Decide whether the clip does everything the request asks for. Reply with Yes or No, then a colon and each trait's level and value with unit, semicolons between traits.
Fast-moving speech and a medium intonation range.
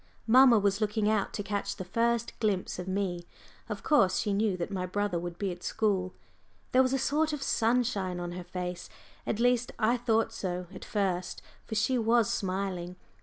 No: average, 190 wpm; average, 4.0 semitones